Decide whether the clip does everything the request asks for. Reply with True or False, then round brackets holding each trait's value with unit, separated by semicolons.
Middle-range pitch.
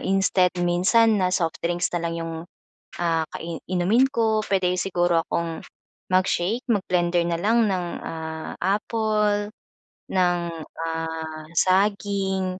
True (180 Hz)